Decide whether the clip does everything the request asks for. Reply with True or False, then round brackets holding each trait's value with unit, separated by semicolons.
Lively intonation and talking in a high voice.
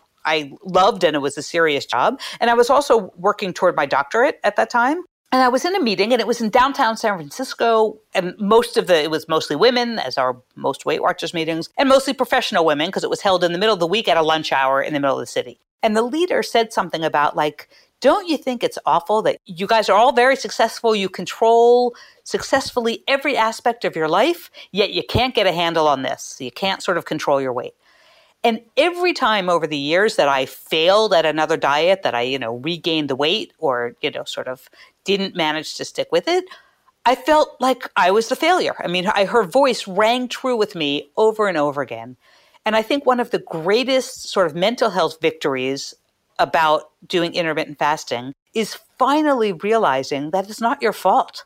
True (7.8 semitones; 210 Hz)